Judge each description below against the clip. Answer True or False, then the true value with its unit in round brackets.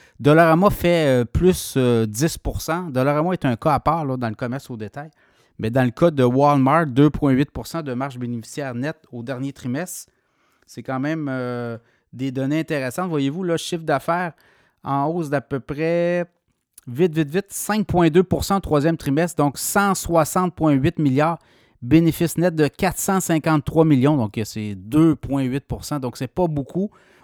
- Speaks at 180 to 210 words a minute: False (155 wpm)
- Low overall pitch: False (150 Hz)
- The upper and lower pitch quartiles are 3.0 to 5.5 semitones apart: True (4.2 semitones)